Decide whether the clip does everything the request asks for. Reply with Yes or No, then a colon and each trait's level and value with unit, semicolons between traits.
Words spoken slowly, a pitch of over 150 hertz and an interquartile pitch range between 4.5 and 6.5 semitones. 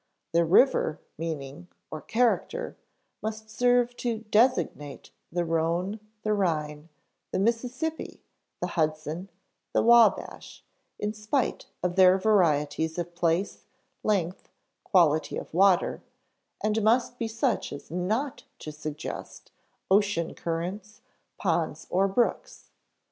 Yes: slow, 110 wpm; medium, 185 Hz; average, 5.0 semitones